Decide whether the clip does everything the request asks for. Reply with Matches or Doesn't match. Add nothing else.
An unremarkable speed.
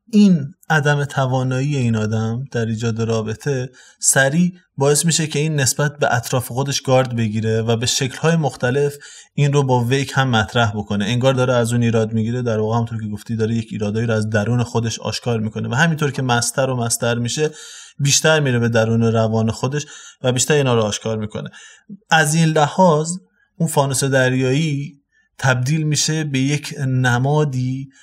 Doesn't match